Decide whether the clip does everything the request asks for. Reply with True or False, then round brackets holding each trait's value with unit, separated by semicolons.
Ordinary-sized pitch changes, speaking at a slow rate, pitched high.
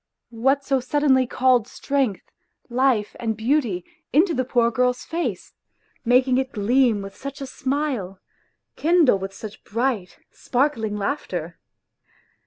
True (4.1 semitones; 125 wpm; 250 Hz)